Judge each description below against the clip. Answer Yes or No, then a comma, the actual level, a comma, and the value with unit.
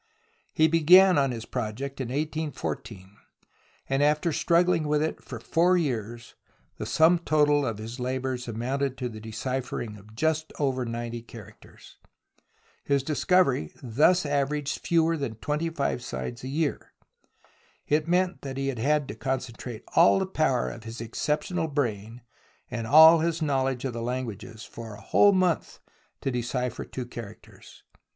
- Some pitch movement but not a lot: Yes, average, 4.8 semitones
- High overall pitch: No, low, 135 Hz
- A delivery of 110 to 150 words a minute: Yes, average, 145 wpm